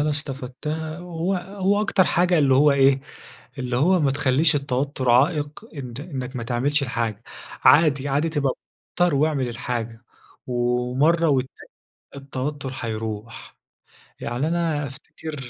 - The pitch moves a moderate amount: Yes, average, 3.9 semitones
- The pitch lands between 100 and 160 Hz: Yes, medium, 140 Hz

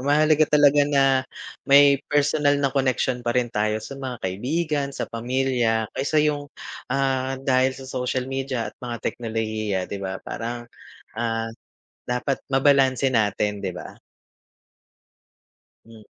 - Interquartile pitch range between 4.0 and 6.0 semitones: No, average, 3.4 semitones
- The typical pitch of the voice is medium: No, low, 130 Hz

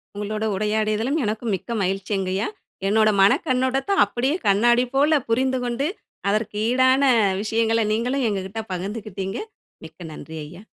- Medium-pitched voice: No, high, 220 Hz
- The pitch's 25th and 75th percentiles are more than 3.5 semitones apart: Yes, average, 4.0 semitones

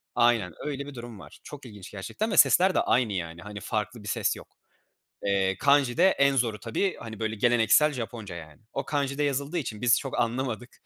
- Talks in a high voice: No, low, 120 Hz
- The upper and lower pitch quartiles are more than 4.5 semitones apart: Yes, average, 5.0 semitones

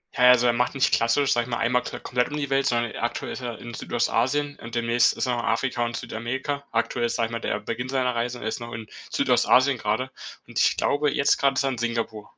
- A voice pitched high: No, low, 120 Hz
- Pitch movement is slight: Yes, narrow, 2.1 semitones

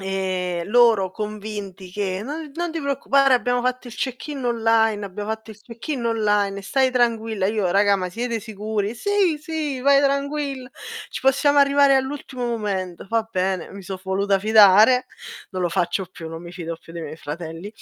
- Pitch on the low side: No, high, 220 Hz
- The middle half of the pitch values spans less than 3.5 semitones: No, average, 5.2 semitones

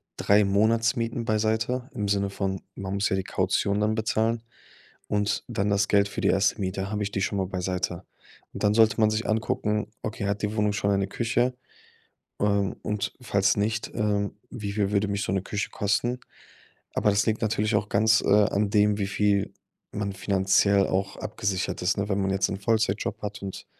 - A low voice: Yes, low, 105 Hz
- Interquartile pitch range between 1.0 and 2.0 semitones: Yes, narrow, 1.6 semitones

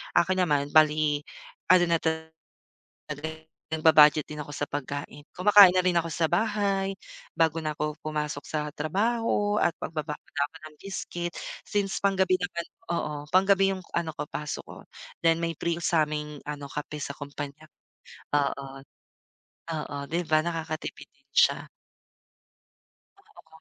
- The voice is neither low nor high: Yes, medium, 160 Hz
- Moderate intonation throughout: Yes, average, 3.4 semitones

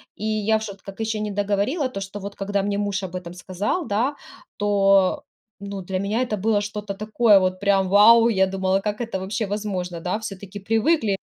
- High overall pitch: Yes, high, 200 Hz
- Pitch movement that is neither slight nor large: No, narrow, 1.8 semitones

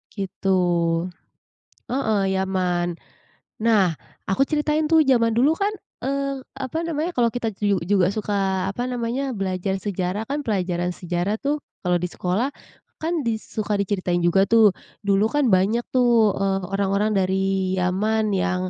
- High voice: Yes, high, 205 Hz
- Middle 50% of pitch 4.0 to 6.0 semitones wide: Yes, average, 4.3 semitones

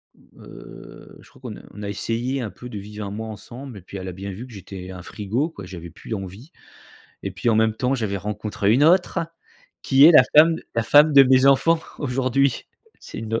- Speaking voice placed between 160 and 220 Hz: No, low, 115 Hz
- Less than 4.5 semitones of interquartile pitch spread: No, average, 5.1 semitones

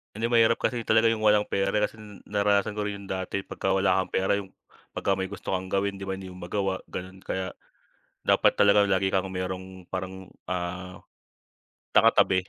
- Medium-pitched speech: No, very low, 95 Hz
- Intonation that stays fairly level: Yes, narrow, 1.5 semitones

